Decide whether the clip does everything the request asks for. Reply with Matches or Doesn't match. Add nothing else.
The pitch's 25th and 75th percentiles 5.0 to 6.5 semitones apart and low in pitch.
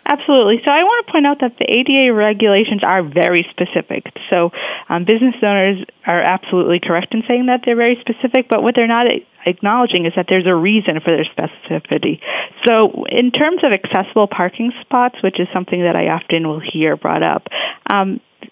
Doesn't match